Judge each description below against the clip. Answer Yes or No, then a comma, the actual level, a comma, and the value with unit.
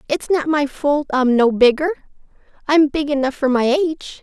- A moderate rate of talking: Yes, average, 185 wpm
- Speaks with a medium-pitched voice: No, very high, 285 Hz